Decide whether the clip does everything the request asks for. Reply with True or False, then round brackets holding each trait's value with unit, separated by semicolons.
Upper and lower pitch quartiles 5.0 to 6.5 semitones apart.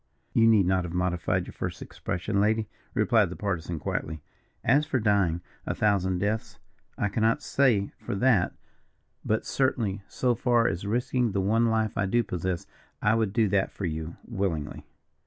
False (3.8 semitones)